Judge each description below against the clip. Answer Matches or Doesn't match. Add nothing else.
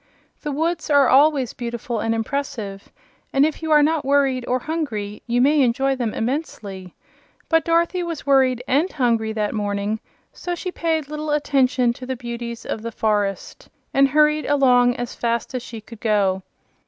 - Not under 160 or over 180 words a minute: Matches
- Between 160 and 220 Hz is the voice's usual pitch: Doesn't match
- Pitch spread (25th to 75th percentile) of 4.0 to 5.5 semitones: Matches